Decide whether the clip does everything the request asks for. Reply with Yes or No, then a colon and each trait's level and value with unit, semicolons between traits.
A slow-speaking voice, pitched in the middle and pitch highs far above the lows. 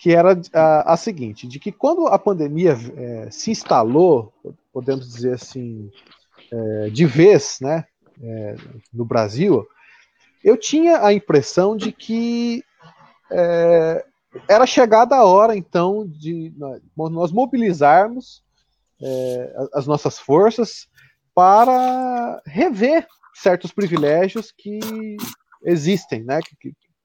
Yes: slow, 115 wpm; medium, 170 Hz; wide, 8.4 semitones